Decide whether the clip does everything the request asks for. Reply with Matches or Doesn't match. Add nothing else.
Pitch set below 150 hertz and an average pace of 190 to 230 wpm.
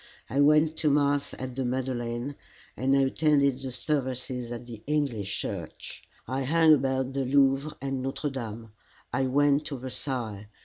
Doesn't match